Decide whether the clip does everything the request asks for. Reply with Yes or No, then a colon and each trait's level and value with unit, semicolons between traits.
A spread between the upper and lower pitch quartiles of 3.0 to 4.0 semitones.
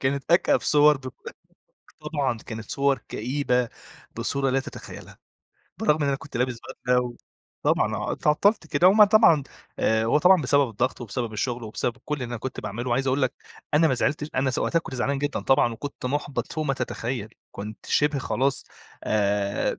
Yes: average, 3.3 semitones